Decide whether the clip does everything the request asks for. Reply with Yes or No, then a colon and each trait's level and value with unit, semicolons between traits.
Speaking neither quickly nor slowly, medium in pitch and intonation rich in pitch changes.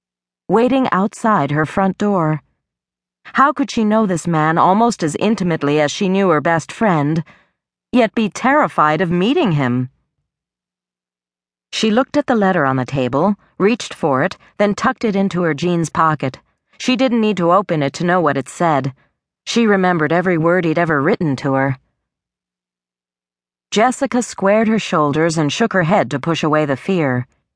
Yes: average, 170 wpm; medium, 170 Hz; wide, 7.0 semitones